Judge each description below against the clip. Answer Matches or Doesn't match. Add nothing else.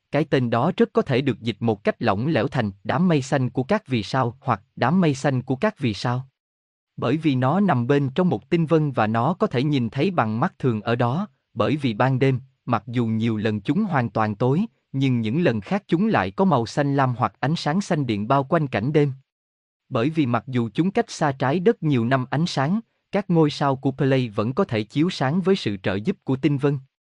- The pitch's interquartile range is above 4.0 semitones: Matches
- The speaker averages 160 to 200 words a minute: Doesn't match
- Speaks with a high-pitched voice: Doesn't match